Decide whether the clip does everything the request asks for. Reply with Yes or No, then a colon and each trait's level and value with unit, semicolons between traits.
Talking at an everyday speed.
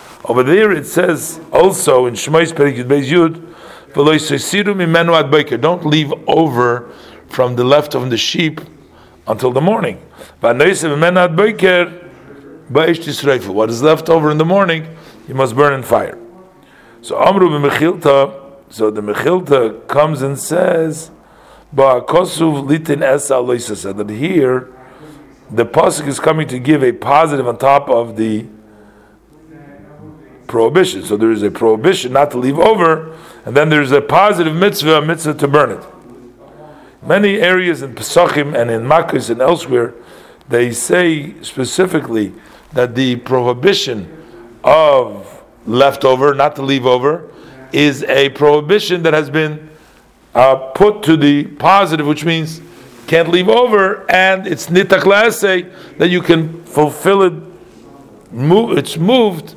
No: slow, 130 wpm